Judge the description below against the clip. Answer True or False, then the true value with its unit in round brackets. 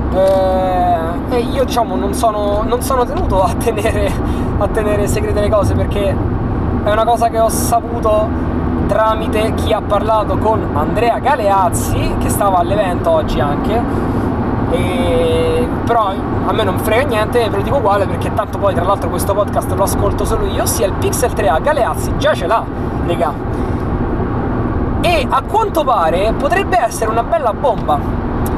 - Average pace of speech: True (155 wpm)